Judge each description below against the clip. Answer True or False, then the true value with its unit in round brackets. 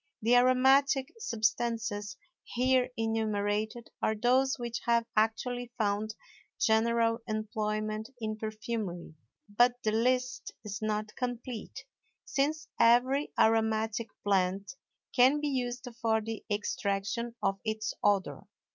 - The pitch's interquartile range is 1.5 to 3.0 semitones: True (2.4 semitones)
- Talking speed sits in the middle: False (110 wpm)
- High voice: True (225 Hz)